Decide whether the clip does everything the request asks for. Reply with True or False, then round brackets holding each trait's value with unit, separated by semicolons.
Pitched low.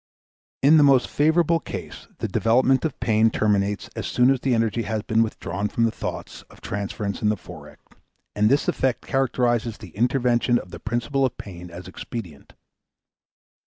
True (115 Hz)